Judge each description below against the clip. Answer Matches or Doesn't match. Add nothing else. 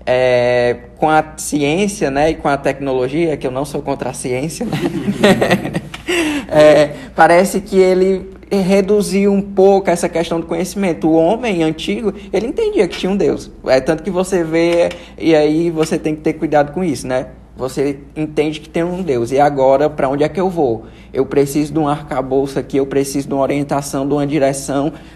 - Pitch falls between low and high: Matches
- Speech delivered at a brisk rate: Matches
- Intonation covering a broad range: Doesn't match